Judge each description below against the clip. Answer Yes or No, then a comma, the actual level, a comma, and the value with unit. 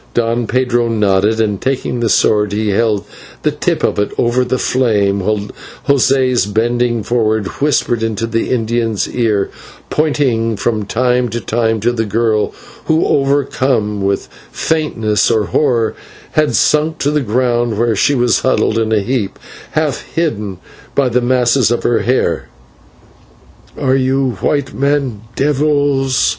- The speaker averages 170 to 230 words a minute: No, average, 150 wpm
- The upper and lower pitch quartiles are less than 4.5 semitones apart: Yes, average, 3.3 semitones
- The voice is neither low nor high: No, low, 120 Hz